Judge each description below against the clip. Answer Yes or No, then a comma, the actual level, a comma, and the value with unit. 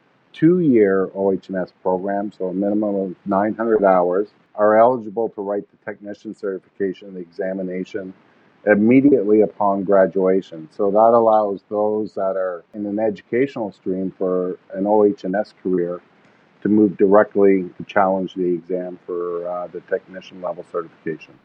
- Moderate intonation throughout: No, narrow, 2.3 semitones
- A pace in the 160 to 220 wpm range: No, slow, 135 wpm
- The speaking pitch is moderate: No, low, 100 Hz